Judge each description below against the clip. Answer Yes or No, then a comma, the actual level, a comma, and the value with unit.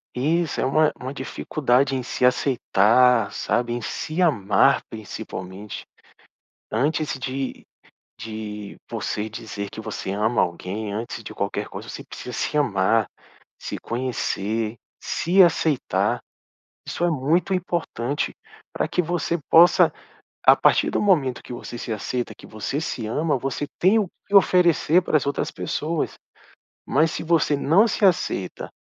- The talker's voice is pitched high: No, low, 130 Hz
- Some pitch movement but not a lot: No, wide, 6.5 semitones